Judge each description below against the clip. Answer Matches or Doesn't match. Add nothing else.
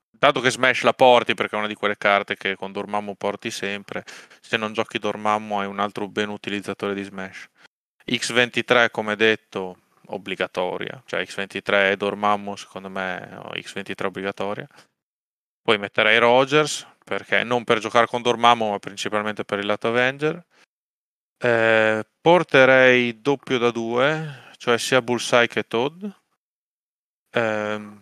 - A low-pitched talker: Matches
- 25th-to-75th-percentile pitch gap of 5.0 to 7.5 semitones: Doesn't match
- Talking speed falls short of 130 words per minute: Doesn't match